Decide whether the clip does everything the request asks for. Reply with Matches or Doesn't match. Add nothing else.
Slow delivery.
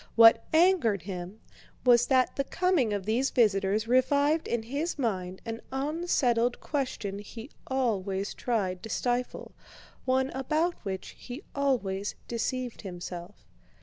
Matches